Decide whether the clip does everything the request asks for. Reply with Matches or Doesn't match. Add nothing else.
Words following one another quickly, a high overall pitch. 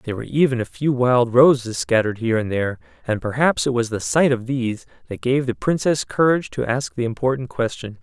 Doesn't match